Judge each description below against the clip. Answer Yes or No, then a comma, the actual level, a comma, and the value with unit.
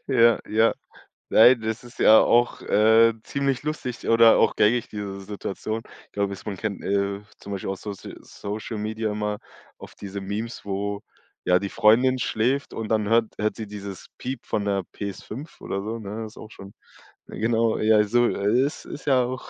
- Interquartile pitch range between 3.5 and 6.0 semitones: No, narrow, 2.4 semitones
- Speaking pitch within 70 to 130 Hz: Yes, low, 110 Hz